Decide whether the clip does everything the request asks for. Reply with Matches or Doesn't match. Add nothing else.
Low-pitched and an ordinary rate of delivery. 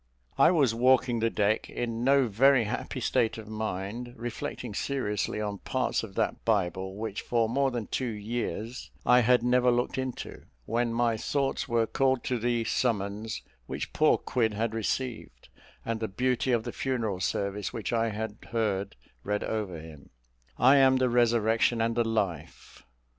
Matches